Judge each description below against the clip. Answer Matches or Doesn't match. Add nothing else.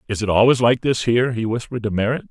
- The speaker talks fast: Matches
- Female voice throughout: Doesn't match